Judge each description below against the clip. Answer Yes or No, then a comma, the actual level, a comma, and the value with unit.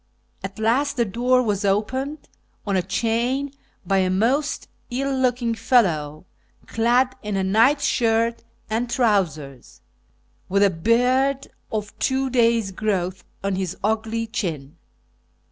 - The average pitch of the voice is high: Yes, high, 225 Hz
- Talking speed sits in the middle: No, slow, 130 wpm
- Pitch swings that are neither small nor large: Yes, average, 4.5 semitones